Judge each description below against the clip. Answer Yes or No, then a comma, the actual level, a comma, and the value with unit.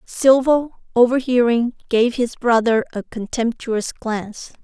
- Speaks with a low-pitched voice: No, high, 240 Hz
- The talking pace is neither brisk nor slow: No, slow, 105 wpm